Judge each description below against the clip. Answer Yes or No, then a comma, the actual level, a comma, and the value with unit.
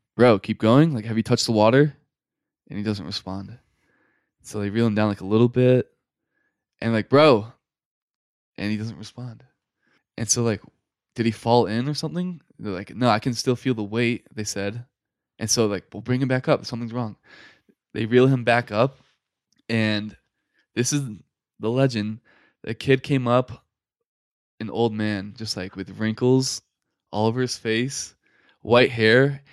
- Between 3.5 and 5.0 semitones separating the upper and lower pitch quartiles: No, average, 3.0 semitones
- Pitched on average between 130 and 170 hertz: No, low, 115 Hz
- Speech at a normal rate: Yes, average, 175 wpm